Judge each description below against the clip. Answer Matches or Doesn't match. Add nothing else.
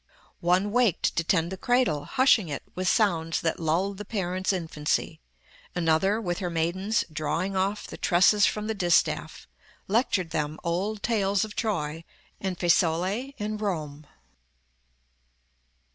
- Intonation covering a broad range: Doesn't match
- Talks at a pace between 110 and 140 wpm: Matches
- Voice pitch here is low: Doesn't match